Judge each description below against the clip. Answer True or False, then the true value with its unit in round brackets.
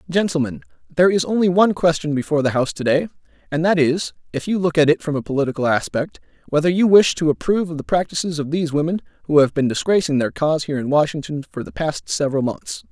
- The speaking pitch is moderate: True (160 Hz)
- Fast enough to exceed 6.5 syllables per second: True (6.8 syllables/s)